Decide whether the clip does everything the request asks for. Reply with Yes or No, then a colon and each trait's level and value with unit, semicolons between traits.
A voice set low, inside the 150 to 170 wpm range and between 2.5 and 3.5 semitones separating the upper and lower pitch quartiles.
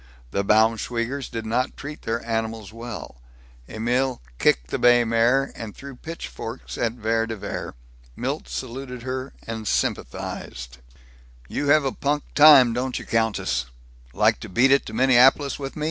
Yes: low, 120 Hz; average, 155 wpm; average, 3.0 semitones